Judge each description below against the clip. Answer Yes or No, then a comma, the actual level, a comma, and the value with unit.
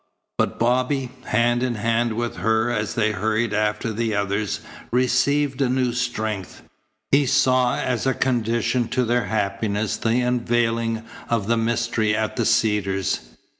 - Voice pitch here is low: Yes, low, 115 Hz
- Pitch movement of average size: No, narrow, 2.3 semitones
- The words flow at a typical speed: Yes, average, 145 wpm